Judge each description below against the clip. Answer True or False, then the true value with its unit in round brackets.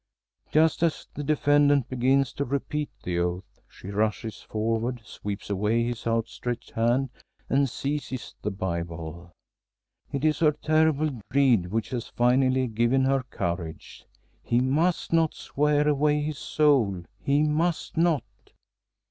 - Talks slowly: True (130 wpm)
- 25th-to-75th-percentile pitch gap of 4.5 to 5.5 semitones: True (5.1 semitones)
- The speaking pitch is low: True (130 Hz)